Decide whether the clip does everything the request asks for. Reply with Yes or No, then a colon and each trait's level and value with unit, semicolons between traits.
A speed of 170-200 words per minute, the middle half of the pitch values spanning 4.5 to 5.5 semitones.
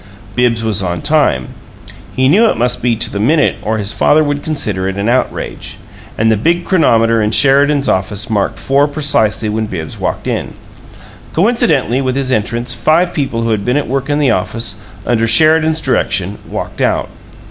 Yes: average, 180 wpm; average, 5.1 semitones